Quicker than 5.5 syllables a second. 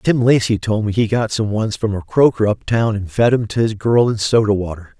No: 5.3 syllables/s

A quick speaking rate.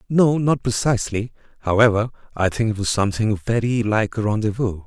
No: average, 160 wpm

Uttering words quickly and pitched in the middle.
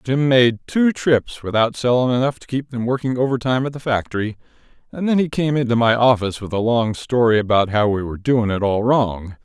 No: fast, 215 wpm; low, 120 Hz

